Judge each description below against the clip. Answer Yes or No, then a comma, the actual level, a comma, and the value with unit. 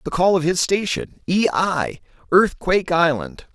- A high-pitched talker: No, medium, 170 Hz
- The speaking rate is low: Yes, slow, 120 wpm